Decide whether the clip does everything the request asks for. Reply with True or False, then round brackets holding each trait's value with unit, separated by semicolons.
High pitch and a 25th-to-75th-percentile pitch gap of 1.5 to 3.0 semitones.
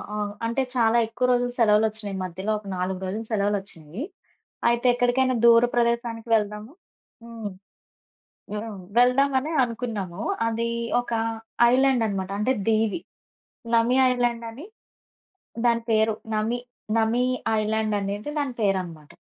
True (225 Hz; 2.7 semitones)